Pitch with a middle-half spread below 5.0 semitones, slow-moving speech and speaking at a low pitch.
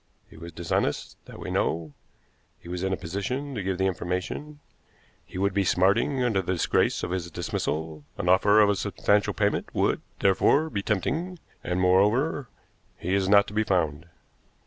No: average, 3.1 semitones; average, 175 wpm; very low, 95 Hz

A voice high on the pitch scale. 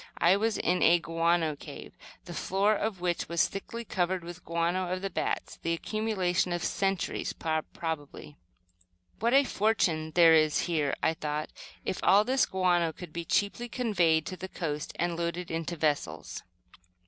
No: medium, 175 Hz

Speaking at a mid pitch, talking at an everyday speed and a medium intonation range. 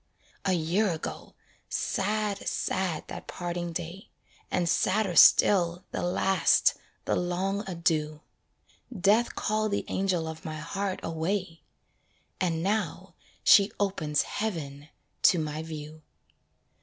No: medium, 175 Hz; slow, 115 wpm; average, 3.5 semitones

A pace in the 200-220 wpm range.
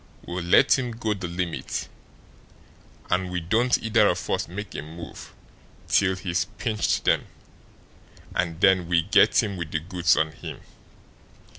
No: average, 150 wpm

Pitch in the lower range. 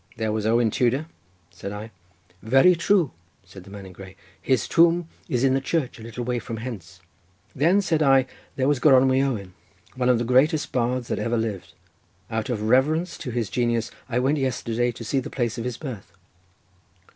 Yes: low, 125 Hz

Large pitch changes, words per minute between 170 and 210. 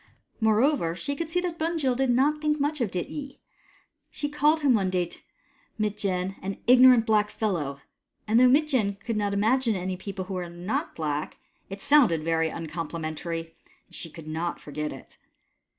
Yes: wide, 7.6 semitones; average, 175 wpm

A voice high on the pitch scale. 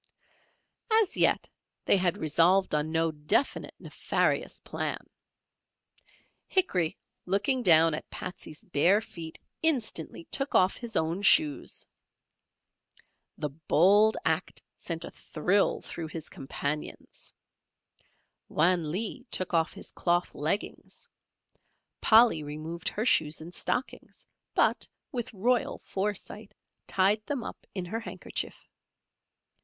No: medium, 180 Hz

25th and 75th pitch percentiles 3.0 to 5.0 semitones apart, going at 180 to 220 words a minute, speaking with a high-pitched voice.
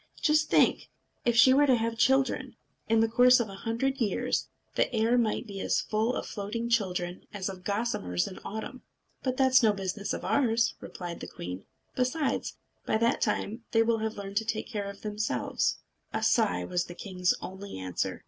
Yes: average, 3.6 semitones; average, 190 wpm; high, 220 Hz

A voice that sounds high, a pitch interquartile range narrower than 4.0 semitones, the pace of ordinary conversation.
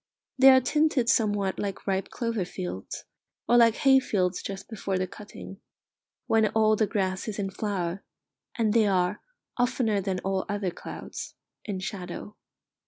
Yes: high, 205 Hz; average, 2.9 semitones; average, 155 wpm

